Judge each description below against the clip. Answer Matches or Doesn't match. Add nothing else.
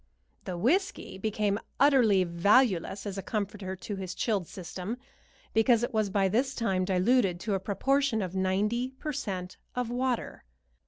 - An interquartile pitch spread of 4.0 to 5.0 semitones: Matches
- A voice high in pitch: Matches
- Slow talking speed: Doesn't match